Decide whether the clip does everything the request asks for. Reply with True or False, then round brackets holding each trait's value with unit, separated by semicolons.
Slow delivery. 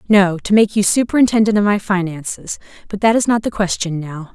False (205 wpm)